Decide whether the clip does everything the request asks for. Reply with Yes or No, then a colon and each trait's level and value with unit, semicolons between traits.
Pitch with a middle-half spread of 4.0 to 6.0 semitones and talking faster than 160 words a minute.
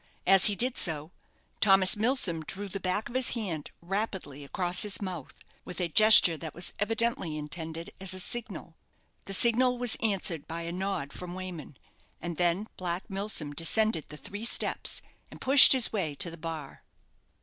Yes: average, 4.5 semitones; average, 170 wpm